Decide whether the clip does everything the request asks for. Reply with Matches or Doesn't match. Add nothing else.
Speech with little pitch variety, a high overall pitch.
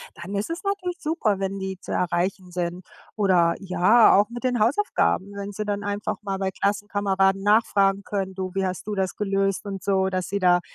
Matches